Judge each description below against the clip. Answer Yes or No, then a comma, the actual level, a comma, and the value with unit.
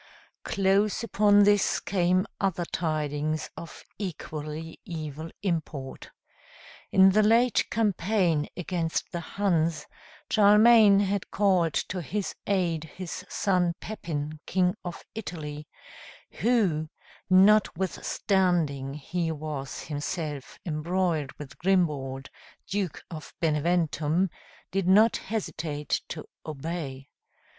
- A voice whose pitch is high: No, medium, 175 Hz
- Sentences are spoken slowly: Yes, slow, 100 wpm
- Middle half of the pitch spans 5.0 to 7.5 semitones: No, average, 4.1 semitones